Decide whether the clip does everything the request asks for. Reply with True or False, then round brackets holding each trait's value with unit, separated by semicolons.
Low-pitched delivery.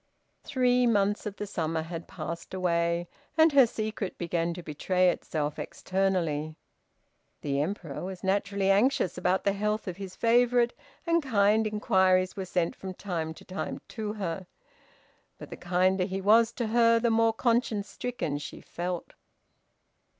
False (195 Hz)